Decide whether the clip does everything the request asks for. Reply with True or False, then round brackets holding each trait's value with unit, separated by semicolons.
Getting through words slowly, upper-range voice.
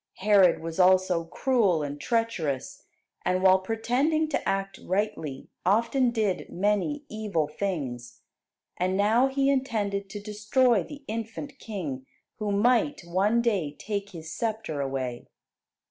True (130 wpm; 200 Hz)